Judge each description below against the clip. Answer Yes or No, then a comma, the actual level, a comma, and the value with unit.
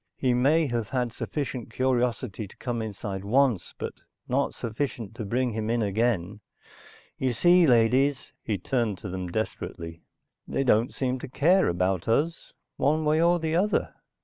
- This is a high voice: No, low, 120 Hz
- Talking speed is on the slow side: No, average, 160 wpm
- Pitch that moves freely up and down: No, average, 4.5 semitones